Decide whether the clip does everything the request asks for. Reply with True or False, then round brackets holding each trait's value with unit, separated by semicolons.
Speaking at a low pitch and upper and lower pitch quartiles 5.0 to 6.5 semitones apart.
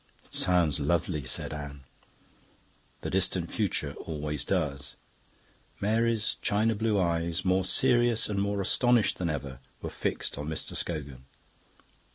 True (85 Hz; 5.6 semitones)